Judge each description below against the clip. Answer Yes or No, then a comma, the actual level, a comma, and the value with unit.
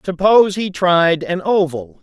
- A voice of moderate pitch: Yes, medium, 180 Hz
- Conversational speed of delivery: Yes, average, 150 wpm